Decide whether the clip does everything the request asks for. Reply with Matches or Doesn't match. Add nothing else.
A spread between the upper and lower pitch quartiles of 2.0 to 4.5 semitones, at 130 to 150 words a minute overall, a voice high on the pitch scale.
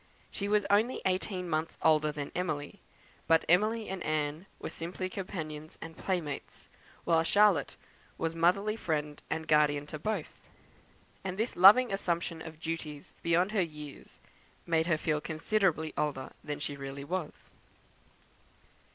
Doesn't match